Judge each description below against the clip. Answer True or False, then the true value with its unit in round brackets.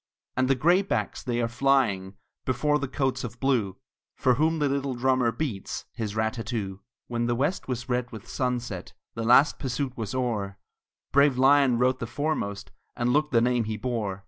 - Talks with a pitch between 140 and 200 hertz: False (125 Hz)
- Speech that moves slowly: False (185 wpm)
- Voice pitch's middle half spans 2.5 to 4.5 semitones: True (3.0 semitones)